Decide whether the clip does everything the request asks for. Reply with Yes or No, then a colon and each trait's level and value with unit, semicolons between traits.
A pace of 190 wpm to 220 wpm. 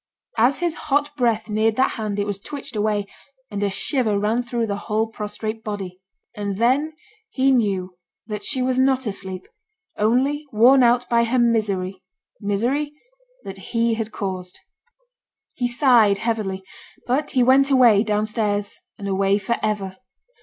No: average, 155 wpm